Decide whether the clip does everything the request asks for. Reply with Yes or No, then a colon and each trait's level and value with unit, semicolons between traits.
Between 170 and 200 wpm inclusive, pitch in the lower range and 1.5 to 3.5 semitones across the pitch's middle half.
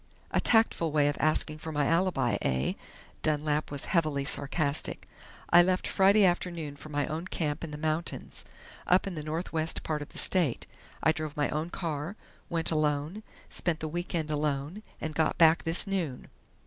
No: average, 175 wpm; medium, 155 Hz; average, 2.7 semitones